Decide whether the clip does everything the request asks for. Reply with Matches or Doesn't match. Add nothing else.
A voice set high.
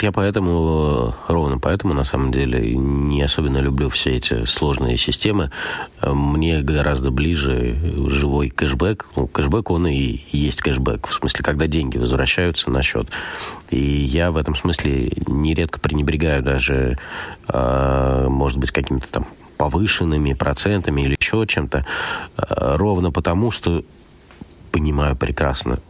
Doesn't match